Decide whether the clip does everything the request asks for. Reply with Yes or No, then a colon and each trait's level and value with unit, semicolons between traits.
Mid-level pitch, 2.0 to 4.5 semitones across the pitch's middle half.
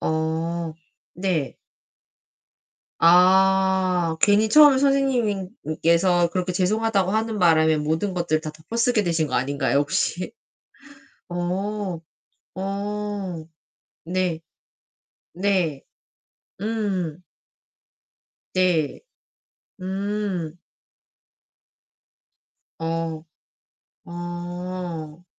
Yes: medium, 180 Hz; average, 3.4 semitones